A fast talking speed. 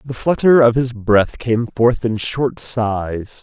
No: average, 175 wpm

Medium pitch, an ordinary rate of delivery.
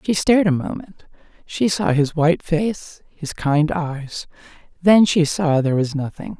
Yes: medium, 175 Hz; average, 160 wpm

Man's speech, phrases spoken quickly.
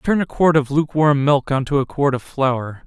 Yes: male; fast, 250 wpm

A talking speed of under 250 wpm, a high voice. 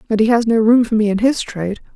No: fast, 305 wpm; high, 225 Hz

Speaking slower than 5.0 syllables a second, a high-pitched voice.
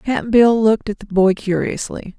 Yes: 4.7 syllables/s; high, 210 Hz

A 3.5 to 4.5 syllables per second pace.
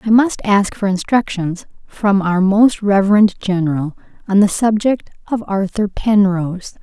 Yes: 4.4 syllables/s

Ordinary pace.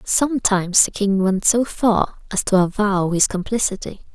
Yes: average, 160 wpm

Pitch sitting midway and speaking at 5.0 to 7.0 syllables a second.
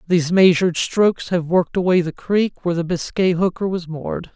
Yes: medium, 175 Hz; 5.7 syllables/s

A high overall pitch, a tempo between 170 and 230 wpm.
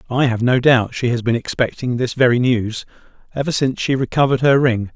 No: low, 125 Hz; fast, 205 wpm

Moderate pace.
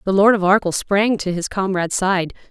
No: fast, 215 wpm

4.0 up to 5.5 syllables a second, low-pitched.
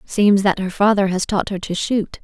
No: 4.7 syllables/s; high, 195 Hz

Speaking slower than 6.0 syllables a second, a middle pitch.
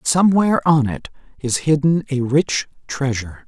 Yes: 4.9 syllables/s; medium, 145 Hz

